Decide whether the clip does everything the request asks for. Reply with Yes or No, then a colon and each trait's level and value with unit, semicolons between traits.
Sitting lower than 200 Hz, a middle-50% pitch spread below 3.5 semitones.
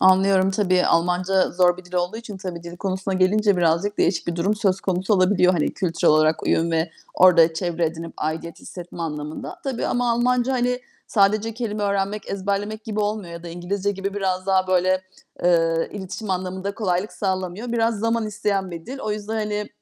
Yes: high, 190 Hz; average, 2.9 semitones